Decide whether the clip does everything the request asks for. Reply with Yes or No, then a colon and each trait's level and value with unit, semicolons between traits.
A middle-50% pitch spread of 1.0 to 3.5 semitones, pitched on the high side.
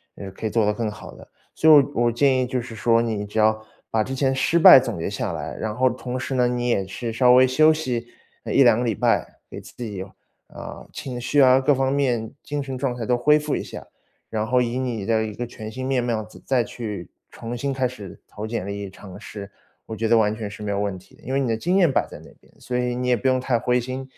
No: average, 3.1 semitones; low, 120 Hz